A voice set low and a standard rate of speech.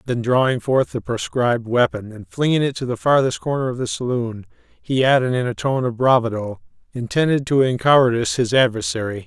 Yes: low, 125 Hz; average, 180 wpm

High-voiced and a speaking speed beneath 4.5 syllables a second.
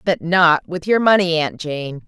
No: medium, 170 Hz; 4.2 syllables/s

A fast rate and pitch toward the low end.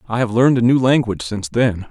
Yes: fast, 250 wpm; low, 115 Hz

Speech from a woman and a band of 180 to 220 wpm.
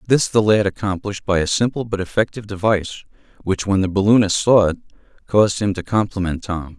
No: male; average, 185 wpm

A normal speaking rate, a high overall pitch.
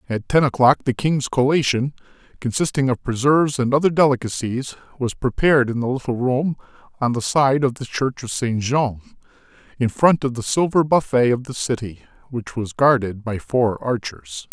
No: average, 175 wpm; low, 125 Hz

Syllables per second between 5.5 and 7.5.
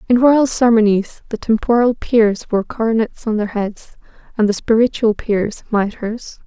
No: 4.5 syllables/s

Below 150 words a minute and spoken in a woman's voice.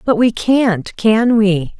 Yes: slow, 135 wpm; female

